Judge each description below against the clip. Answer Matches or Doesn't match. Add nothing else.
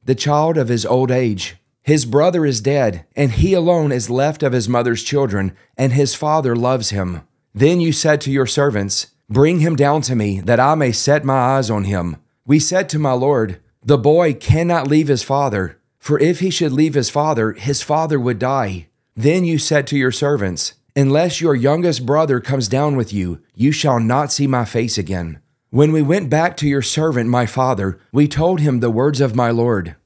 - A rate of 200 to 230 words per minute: Matches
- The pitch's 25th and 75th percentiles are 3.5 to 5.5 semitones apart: Matches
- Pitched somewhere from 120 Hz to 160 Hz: Matches